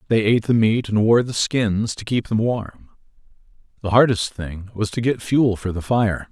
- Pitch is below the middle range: Yes, low, 110 Hz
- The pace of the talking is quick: Yes, fast, 210 wpm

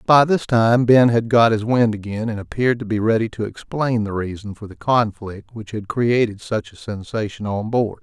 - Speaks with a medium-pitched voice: No, low, 110 Hz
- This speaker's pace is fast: Yes, fast, 215 wpm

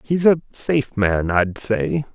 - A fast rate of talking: No, average, 170 wpm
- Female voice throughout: No, male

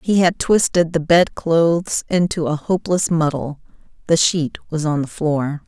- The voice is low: No, medium, 165 Hz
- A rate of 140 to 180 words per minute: Yes, average, 170 wpm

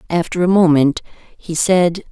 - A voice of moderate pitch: Yes, medium, 170 Hz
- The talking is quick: No, average, 140 wpm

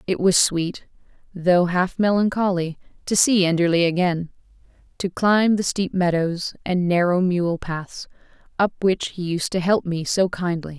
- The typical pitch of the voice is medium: Yes, medium, 180 Hz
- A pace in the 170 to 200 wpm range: No, average, 155 wpm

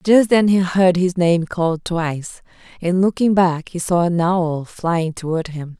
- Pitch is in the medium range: Yes, medium, 175 Hz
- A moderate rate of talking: Yes, average, 185 wpm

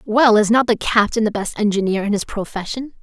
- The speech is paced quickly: Yes, fast, 220 wpm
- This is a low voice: No, high, 215 Hz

